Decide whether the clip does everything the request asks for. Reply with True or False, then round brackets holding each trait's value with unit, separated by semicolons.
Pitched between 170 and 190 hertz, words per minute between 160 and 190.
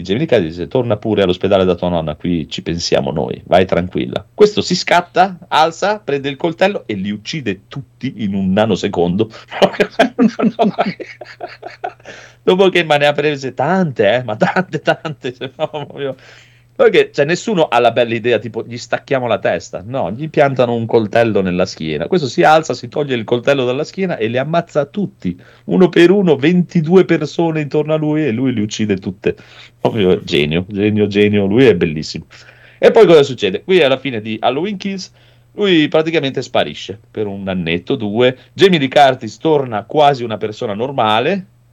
False (135 Hz; 165 wpm)